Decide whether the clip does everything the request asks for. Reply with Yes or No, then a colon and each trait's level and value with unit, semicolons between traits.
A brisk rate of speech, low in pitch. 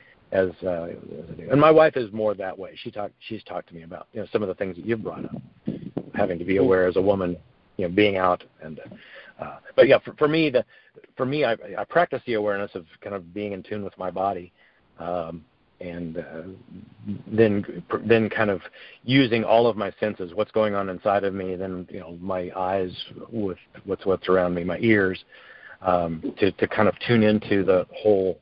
Yes: fast, 220 wpm; low, 100 Hz